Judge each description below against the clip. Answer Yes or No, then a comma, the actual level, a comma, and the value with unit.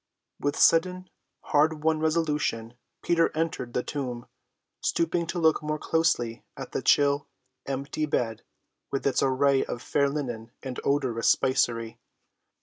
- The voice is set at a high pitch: No, medium, 140 Hz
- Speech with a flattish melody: No, average, 4.2 semitones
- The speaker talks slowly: Yes, slow, 130 wpm